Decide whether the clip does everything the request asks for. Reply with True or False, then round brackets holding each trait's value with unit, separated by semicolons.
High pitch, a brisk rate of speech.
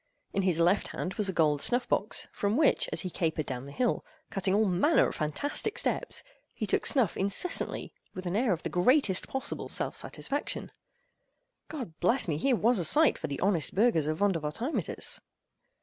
False (195 Hz; 180 wpm)